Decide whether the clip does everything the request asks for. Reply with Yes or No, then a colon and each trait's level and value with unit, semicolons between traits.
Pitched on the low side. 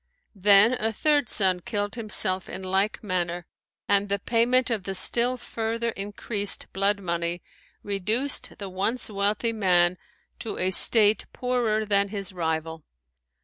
No: high, 205 Hz